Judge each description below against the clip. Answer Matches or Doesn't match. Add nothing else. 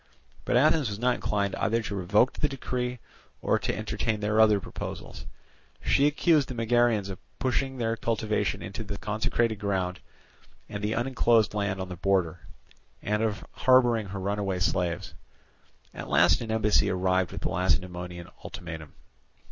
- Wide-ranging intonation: Doesn't match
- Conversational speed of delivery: Matches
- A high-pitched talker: Doesn't match